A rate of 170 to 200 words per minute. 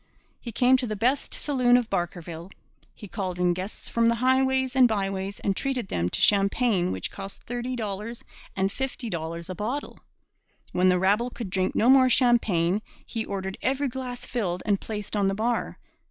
Yes: average, 185 wpm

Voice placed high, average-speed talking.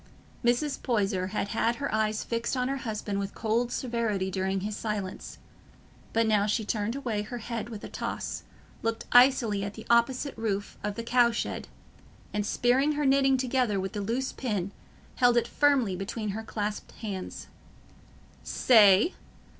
Yes: high, 225 Hz; average, 160 wpm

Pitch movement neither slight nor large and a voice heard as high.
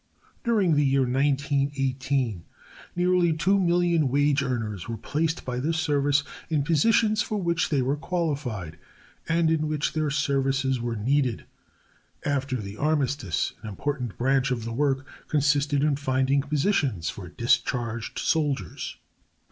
No: average, 3.4 semitones; medium, 140 Hz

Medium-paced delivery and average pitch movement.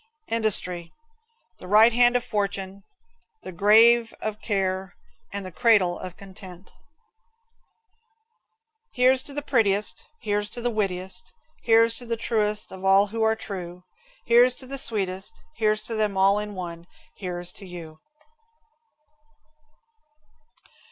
No: slow, 130 wpm; average, 3.3 semitones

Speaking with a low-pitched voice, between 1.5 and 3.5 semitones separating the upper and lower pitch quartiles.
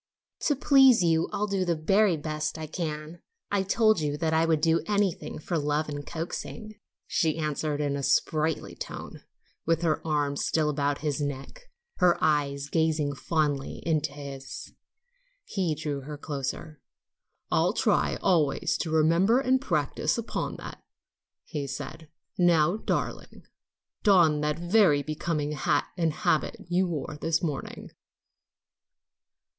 No: medium, 155 Hz; average, 2.9 semitones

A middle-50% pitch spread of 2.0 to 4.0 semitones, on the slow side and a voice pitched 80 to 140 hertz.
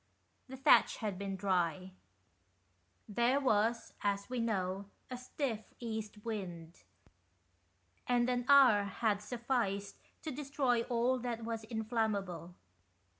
No: average, 3.6 semitones; slow, 115 wpm; high, 220 Hz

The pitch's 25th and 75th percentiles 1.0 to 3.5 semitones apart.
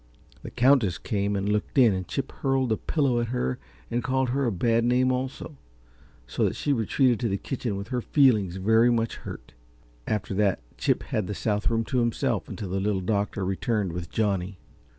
No: average, 4.1 semitones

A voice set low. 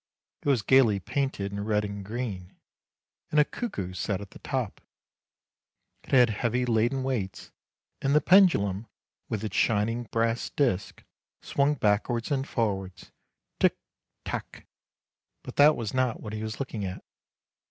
Yes: low, 115 Hz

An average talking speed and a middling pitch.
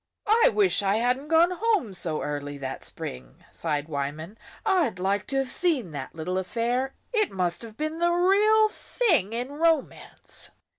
No: average, 160 wpm; high, 245 Hz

